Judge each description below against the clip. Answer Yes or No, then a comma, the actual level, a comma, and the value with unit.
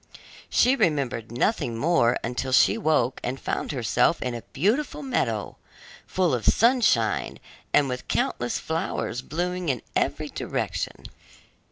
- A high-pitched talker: No, low, 135 Hz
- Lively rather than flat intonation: Yes, wide, 6.8 semitones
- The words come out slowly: Yes, slow, 130 wpm